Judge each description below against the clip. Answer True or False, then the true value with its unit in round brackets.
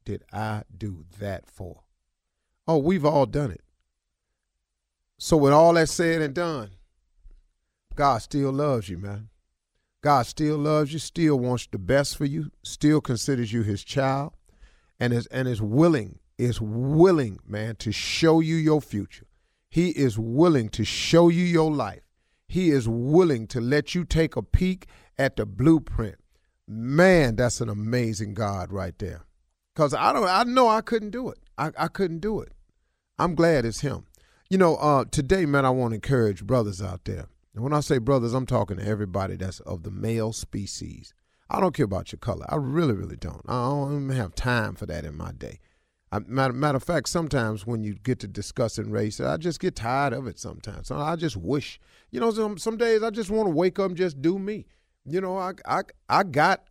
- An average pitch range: False (7.4 semitones)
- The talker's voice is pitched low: True (125 Hz)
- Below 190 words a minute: False (195 wpm)